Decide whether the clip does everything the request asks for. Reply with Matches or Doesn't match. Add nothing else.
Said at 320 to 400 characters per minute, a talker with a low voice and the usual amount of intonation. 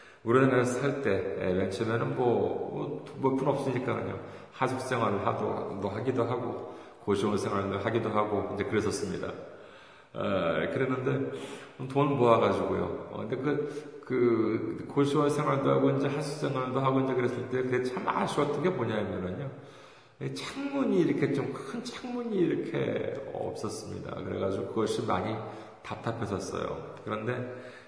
Doesn't match